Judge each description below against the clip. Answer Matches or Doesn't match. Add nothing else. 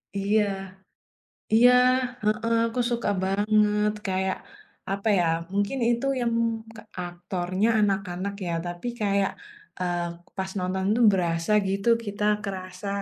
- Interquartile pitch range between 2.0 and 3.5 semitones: Matches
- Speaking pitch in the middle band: Doesn't match